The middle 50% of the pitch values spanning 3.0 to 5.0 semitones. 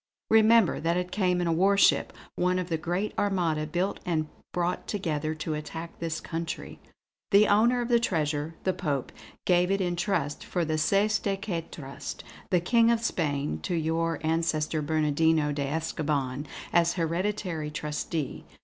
Yes: average, 3.4 semitones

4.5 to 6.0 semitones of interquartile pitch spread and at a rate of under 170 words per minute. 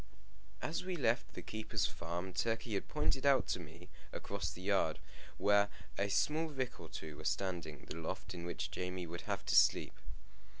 No: average, 5.1 semitones; average, 180 wpm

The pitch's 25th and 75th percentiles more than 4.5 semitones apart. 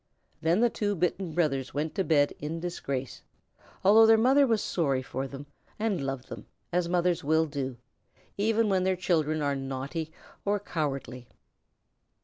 Yes: wide, 5.6 semitones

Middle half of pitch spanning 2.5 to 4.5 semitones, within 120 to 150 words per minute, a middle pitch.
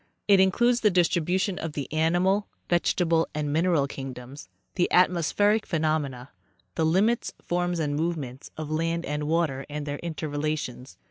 Yes: average, 3.3 semitones; average, 140 wpm; medium, 160 Hz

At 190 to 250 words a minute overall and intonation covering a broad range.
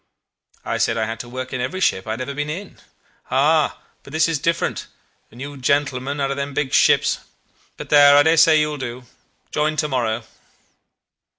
No: average, 200 wpm; average, 3.0 semitones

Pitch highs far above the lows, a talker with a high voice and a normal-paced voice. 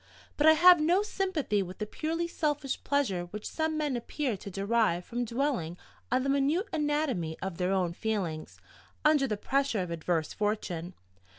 Yes: wide, 8.3 semitones; high, 240 Hz; average, 170 wpm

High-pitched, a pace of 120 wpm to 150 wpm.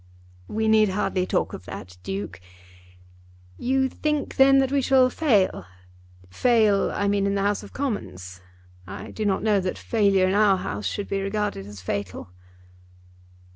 No: high, 200 Hz; average, 160 wpm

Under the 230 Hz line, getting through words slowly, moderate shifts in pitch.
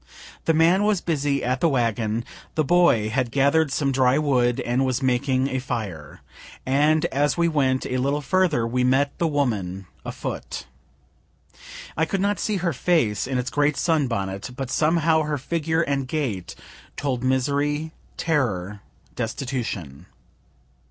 No: low, 135 Hz; average, 150 wpm; average, 4.1 semitones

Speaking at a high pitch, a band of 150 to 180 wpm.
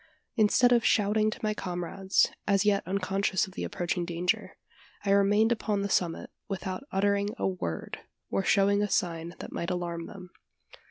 Yes: high, 195 Hz; average, 165 wpm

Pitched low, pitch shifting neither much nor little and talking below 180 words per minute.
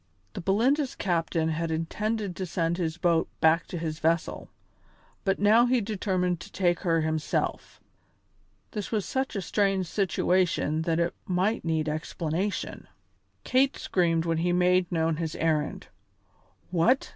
No: medium, 175 Hz; average, 3.4 semitones; average, 145 wpm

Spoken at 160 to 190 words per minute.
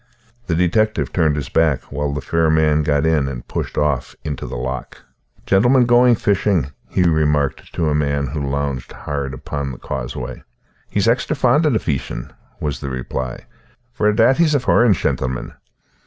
Yes: average, 180 wpm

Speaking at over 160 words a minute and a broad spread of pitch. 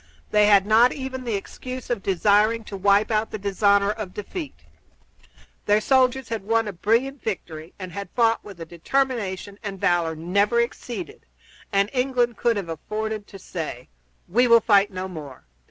No: average, 170 wpm; average, 3.4 semitones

